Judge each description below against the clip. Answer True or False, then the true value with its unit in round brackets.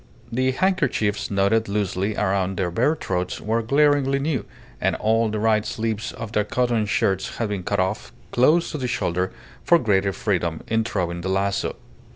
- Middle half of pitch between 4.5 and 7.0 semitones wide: False (4.0 semitones)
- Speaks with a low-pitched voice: True (105 Hz)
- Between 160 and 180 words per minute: True (175 wpm)